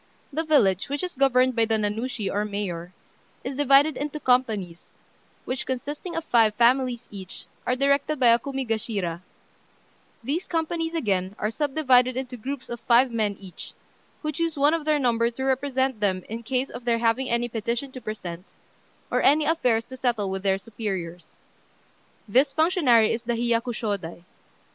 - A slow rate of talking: No, average, 160 wpm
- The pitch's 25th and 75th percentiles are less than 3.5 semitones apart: No, average, 4.3 semitones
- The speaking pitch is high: Yes, high, 240 Hz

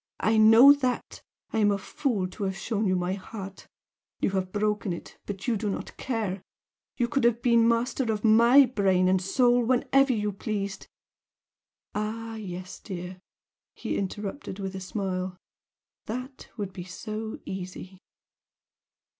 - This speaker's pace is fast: No, average, 155 wpm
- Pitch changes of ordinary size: Yes, average, 3.5 semitones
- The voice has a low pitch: No, high, 210 Hz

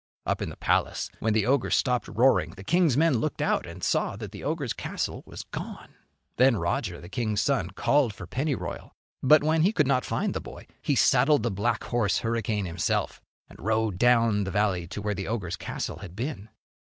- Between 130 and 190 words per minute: No, fast, 205 wpm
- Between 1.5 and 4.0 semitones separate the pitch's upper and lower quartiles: No, average, 5.1 semitones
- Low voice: Yes, low, 115 Hz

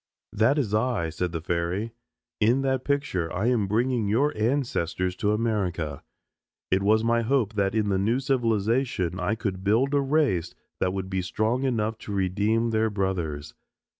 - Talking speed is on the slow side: No, average, 165 wpm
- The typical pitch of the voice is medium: No, low, 110 Hz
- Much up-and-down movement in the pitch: No, average, 4.2 semitones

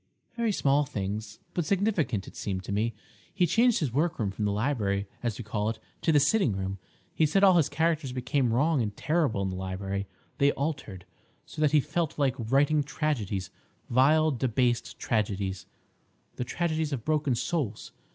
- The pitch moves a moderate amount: No, wide, 6.8 semitones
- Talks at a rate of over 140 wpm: Yes, average, 170 wpm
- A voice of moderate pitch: No, low, 130 Hz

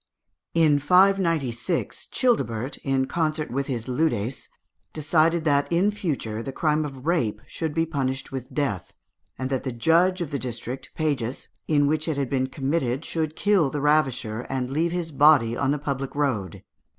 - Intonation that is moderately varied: Yes, average, 3.7 semitones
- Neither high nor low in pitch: Yes, medium, 145 Hz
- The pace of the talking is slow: No, average, 165 wpm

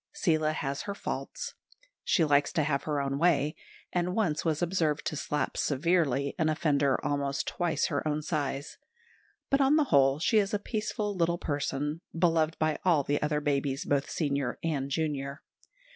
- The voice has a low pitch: No, medium, 150 Hz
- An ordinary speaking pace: Yes, average, 170 wpm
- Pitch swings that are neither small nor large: Yes, average, 3.3 semitones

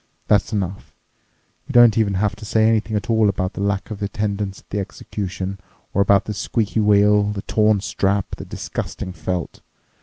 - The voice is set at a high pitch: No, low, 100 Hz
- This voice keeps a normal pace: Yes, average, 180 wpm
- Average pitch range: No, narrow, 1.5 semitones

